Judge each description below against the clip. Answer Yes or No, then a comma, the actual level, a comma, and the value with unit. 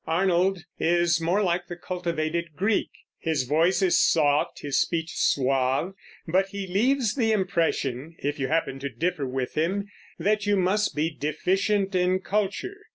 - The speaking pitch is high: No, medium, 175 Hz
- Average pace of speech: Yes, average, 155 wpm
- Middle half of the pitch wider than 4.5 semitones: No, average, 4.0 semitones